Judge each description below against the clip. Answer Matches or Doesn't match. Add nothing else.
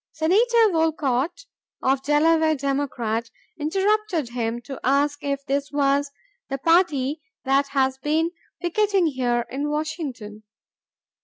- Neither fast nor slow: Doesn't match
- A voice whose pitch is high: Matches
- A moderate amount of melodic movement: Matches